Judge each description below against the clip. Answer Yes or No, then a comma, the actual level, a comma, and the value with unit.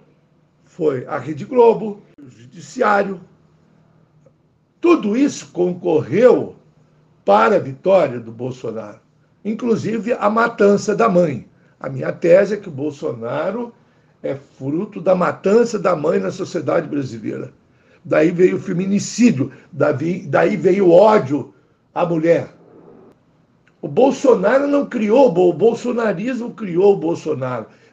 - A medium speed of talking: No, slow, 115 wpm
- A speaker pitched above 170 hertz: Yes, medium, 185 Hz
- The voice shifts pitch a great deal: Yes, wide, 6.0 semitones